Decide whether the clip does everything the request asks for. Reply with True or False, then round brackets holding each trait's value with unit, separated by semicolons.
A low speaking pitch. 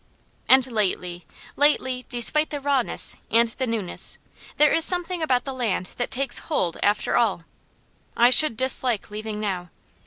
False (245 Hz)